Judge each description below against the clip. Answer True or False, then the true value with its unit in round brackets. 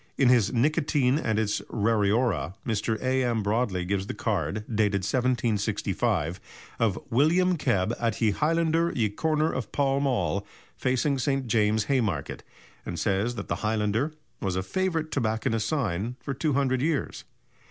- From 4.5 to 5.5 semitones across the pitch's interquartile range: True (4.9 semitones)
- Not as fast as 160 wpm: True (140 wpm)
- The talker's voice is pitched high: False (115 Hz)